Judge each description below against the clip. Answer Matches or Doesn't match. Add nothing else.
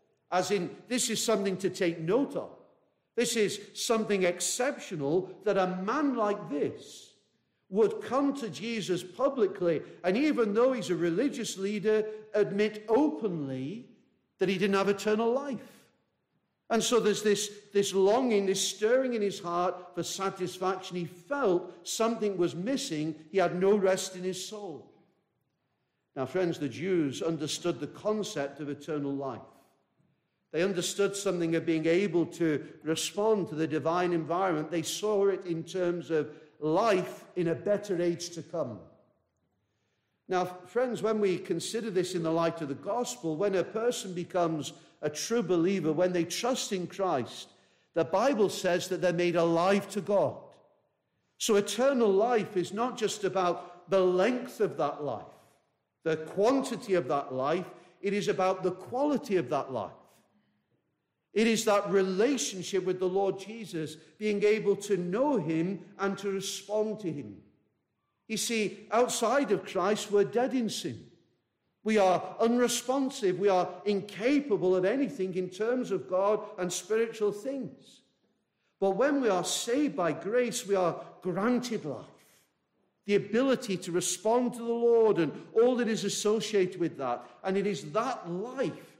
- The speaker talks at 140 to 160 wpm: Matches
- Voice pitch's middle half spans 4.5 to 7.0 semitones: Doesn't match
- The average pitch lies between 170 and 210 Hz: Matches